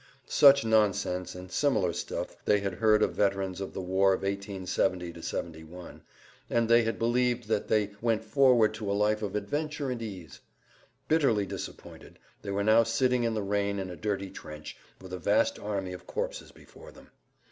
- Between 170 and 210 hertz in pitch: No, low, 105 Hz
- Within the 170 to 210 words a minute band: Yes, average, 180 wpm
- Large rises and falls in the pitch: No, average, 3.3 semitones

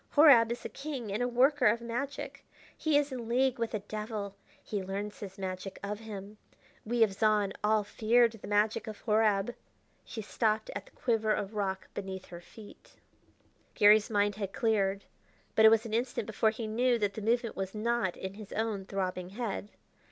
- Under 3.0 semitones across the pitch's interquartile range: Yes, narrow, 2.6 semitones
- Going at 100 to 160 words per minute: No, average, 190 wpm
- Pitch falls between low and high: No, high, 215 Hz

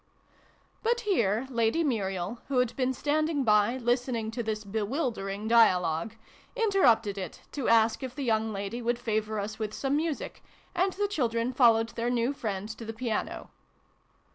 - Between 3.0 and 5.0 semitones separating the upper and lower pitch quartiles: Yes, average, 3.4 semitones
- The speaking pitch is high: Yes, high, 230 Hz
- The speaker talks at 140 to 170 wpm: Yes, average, 165 wpm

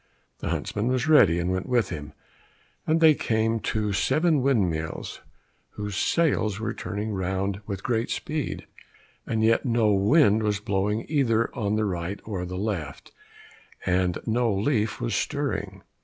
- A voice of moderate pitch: No, low, 105 Hz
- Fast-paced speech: No, average, 150 wpm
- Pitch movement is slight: No, average, 3.5 semitones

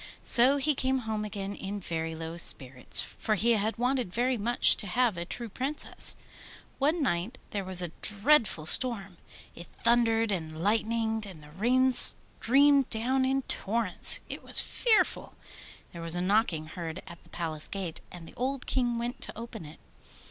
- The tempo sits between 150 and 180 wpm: Yes, average, 170 wpm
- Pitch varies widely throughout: Yes, wide, 6.0 semitones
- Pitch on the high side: Yes, high, 220 Hz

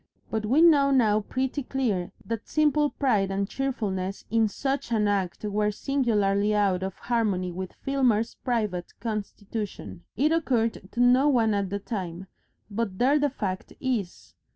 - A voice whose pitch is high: Yes, high, 220 Hz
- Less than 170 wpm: Yes, average, 155 wpm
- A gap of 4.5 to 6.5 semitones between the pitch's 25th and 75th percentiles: Yes, average, 4.8 semitones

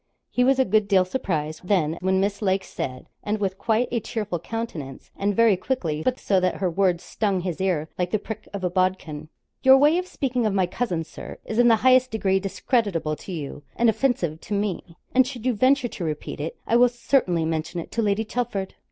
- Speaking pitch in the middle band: No, high, 200 Hz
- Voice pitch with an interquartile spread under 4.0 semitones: No, average, 5.0 semitones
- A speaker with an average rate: No, fast, 220 wpm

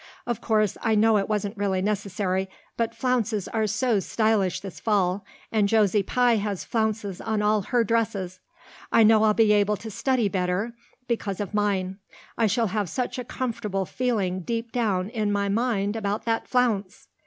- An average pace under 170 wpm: No, average, 175 wpm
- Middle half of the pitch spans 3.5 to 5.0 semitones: No, narrow, 2.4 semitones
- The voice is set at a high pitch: Yes, high, 210 Hz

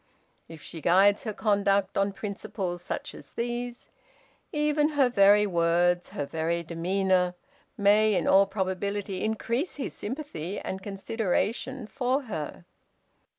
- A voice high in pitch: Yes, high, 200 Hz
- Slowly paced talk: Yes, slow, 125 wpm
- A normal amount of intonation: Yes, average, 4.4 semitones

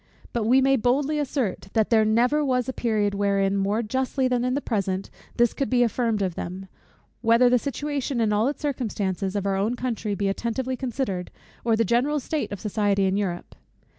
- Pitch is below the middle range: No, high, 230 Hz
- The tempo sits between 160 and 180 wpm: No, average, 195 wpm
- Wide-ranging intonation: No, average, 4.3 semitones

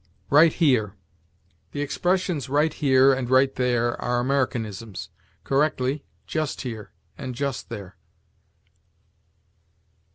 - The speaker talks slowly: Yes, slow, 100 wpm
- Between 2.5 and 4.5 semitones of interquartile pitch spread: Yes, average, 3.2 semitones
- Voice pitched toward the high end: No, low, 130 Hz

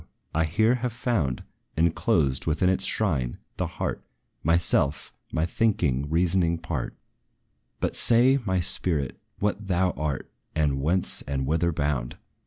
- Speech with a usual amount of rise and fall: Yes, average, 4.6 semitones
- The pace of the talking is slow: Yes, slow, 130 wpm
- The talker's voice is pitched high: No, very low, 85 Hz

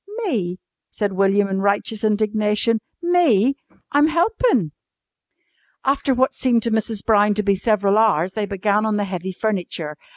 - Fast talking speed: No, average, 150 wpm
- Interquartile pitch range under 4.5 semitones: Yes, average, 2.8 semitones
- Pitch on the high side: Yes, high, 210 Hz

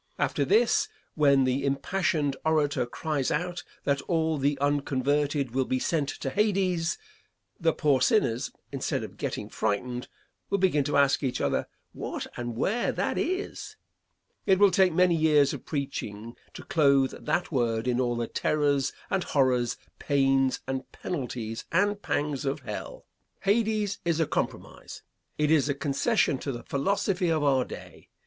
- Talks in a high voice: No, medium, 145 Hz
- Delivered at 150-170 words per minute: Yes, average, 155 wpm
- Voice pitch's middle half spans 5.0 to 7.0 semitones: No, average, 4.4 semitones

